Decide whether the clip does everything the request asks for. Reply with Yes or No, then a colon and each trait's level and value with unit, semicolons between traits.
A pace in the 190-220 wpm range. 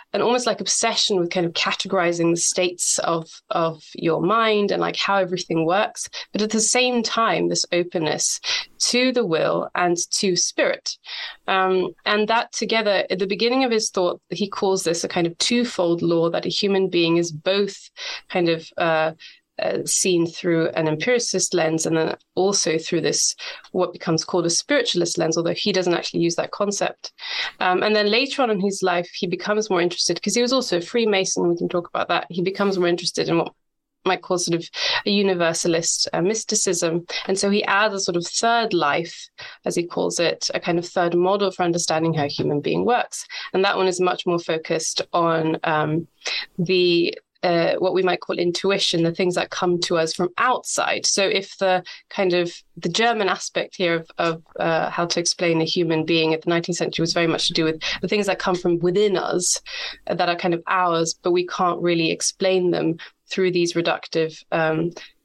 Yes: average, 200 wpm